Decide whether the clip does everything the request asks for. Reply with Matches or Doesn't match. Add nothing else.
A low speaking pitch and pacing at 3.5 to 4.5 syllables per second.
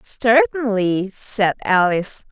Doesn't match